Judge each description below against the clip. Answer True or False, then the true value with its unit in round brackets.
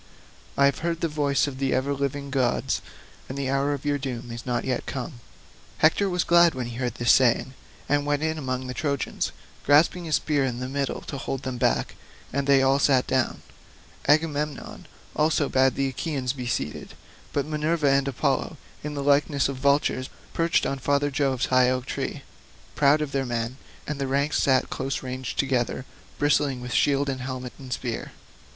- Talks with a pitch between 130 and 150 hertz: True (135 Hz)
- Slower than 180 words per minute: False (190 wpm)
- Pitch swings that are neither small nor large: False (2.1 semitones)